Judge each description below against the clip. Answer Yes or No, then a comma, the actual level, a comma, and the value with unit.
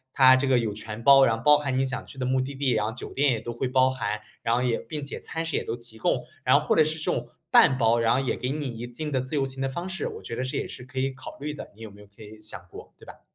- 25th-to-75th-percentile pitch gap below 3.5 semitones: Yes, average, 2.9 semitones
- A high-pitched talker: No, low, 130 Hz